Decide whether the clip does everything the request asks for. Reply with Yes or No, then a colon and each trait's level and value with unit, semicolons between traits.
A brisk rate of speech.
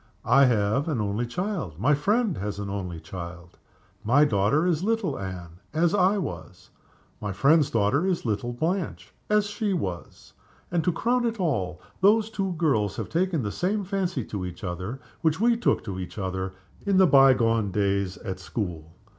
No: average, 180 wpm